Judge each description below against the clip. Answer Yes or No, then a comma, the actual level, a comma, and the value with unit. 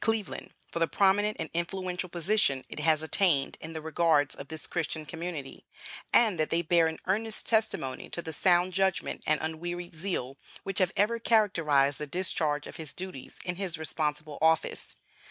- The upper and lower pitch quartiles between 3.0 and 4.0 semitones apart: Yes, average, 3.5 semitones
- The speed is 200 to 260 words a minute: No, average, 175 wpm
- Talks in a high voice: No, medium, 170 Hz